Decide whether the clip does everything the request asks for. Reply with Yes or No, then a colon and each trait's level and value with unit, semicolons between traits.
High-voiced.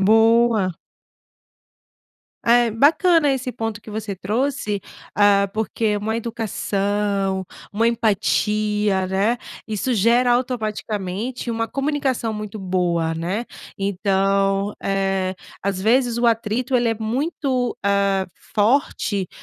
Yes: high, 215 Hz